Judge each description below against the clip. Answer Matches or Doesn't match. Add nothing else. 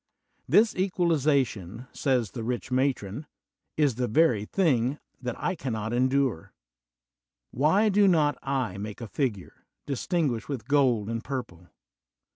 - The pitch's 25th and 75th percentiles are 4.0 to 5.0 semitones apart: Matches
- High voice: Doesn't match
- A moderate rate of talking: Doesn't match